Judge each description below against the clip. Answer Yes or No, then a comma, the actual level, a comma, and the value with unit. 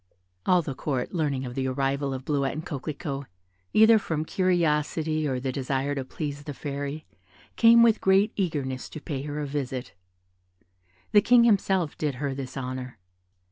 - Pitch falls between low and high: Yes, medium, 145 Hz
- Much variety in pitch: No, average, 3.5 semitones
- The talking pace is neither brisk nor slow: Yes, average, 160 wpm